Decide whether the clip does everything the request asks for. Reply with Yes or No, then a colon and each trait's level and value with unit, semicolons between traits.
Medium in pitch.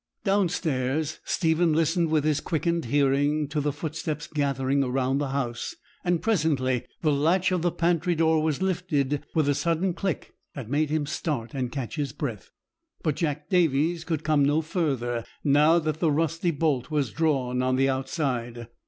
Yes: medium, 150 Hz